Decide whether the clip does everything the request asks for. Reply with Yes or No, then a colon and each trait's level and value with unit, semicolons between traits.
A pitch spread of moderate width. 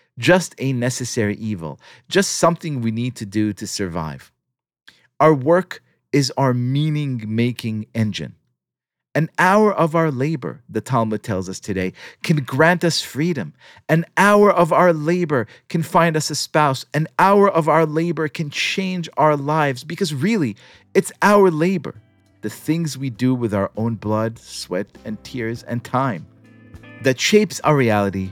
No: wide, 6.8 semitones